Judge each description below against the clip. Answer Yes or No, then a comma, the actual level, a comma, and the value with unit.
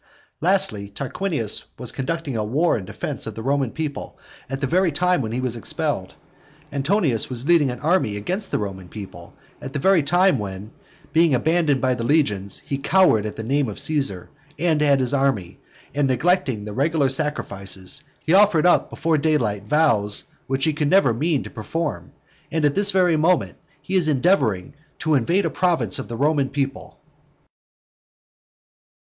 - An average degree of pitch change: No, wide, 6.1 semitones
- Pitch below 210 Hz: Yes, medium, 140 Hz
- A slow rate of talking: No, average, 170 wpm